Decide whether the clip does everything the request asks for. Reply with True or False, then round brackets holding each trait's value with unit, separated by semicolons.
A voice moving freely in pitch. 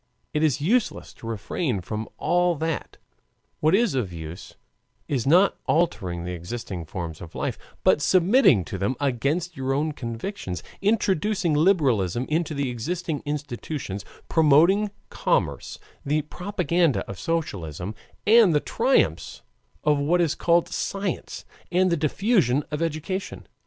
True (7.4 semitones)